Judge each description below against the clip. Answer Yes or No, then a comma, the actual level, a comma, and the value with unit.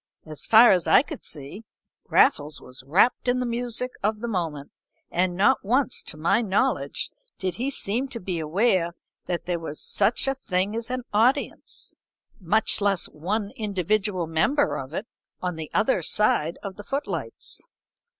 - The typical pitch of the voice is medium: No, high, 200 Hz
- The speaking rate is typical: Yes, average, 165 wpm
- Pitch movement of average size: No, wide, 5.8 semitones